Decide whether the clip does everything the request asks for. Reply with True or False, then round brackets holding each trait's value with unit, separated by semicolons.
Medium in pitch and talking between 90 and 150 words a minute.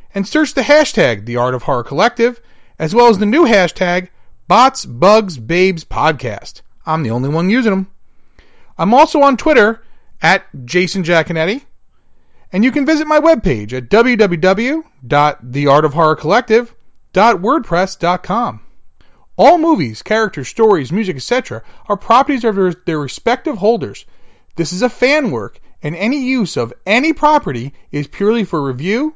False (195 Hz; 140 wpm)